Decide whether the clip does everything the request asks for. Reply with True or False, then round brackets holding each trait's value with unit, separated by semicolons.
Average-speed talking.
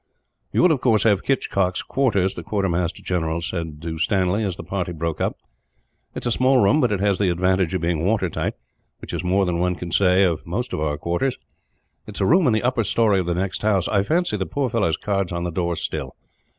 False (240 wpm)